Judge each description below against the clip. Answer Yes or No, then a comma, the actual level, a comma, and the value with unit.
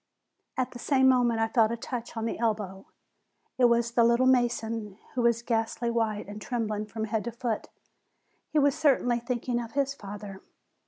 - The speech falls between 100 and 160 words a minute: No, average, 190 wpm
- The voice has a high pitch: Yes, high, 235 Hz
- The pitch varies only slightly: Yes, narrow, 1.9 semitones